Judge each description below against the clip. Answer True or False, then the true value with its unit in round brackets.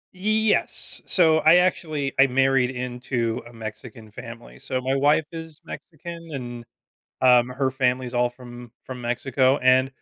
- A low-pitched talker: True (130 Hz)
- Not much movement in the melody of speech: False (3.3 semitones)